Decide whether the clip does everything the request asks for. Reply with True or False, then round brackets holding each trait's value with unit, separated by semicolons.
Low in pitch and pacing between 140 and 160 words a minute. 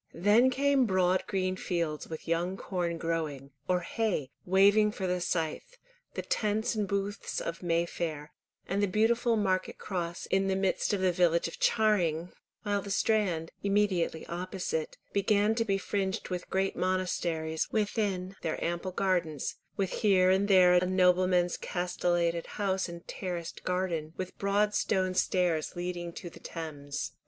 False (185 Hz; 155 wpm)